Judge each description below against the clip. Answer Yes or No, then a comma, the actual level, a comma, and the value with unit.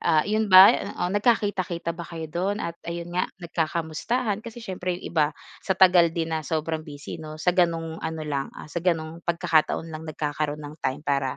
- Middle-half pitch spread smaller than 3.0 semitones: Yes, narrow, 2.6 semitones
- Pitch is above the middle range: No, medium, 165 Hz